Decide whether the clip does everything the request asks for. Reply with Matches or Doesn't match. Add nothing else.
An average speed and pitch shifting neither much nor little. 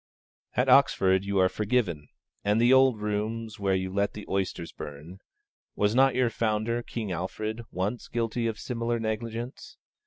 Matches